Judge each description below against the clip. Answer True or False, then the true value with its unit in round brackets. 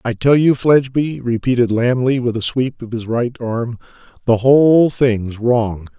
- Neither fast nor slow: True (170 wpm)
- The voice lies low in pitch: True (120 Hz)